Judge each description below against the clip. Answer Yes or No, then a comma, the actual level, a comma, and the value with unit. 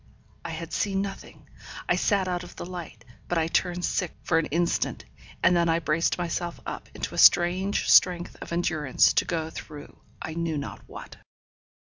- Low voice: No, medium, 170 Hz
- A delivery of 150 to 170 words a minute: No, average, 180 wpm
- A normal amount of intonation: No, narrow, 1.8 semitones